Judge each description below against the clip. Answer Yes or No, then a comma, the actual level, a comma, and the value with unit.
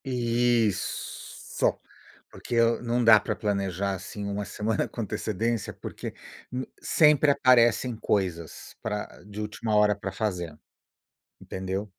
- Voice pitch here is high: No, low, 105 Hz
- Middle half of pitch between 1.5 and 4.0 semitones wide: Yes, average, 3.0 semitones